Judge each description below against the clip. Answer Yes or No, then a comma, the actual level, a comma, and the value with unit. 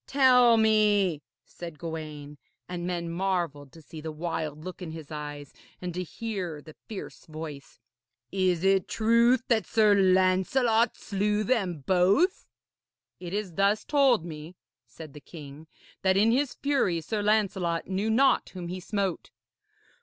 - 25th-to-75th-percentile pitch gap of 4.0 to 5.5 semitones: Yes, average, 4.8 semitones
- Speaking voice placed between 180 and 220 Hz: Yes, medium, 185 Hz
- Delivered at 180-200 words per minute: No, average, 145 wpm